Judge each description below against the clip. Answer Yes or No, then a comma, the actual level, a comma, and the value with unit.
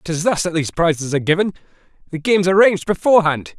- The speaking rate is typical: Yes, average, 185 wpm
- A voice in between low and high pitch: Yes, medium, 170 Hz